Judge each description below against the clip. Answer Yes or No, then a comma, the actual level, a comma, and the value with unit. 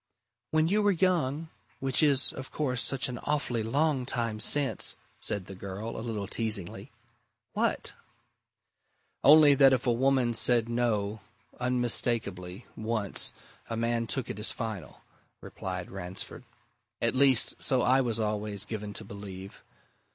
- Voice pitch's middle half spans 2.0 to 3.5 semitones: No, average, 4.1 semitones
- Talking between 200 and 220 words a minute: No, average, 140 wpm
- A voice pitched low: Yes, low, 115 Hz